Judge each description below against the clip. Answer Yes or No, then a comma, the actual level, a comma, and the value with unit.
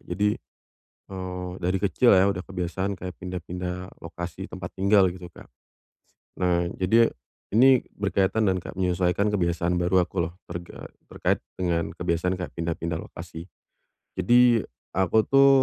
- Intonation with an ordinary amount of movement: No, narrow, 1.9 semitones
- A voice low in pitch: Yes, very low, 90 Hz